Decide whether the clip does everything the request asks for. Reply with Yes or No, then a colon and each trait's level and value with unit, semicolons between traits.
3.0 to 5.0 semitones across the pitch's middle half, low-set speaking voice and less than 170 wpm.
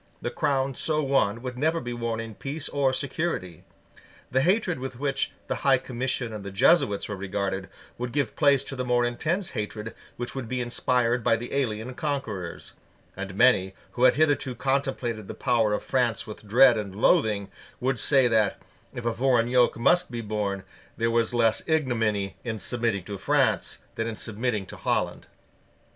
No: average, 3.7 semitones; low, 120 Hz; average, 180 wpm